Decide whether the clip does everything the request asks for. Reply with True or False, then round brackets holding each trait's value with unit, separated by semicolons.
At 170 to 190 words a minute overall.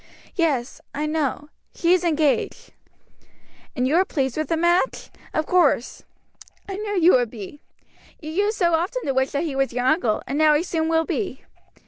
True (185 wpm)